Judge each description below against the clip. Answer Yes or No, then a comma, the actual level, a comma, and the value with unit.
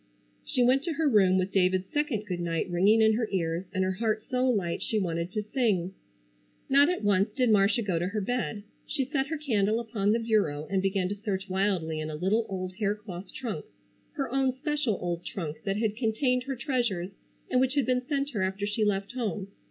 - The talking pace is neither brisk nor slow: No, fast, 215 wpm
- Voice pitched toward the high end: Yes, high, 210 Hz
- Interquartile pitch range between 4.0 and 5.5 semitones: Yes, average, 4.9 semitones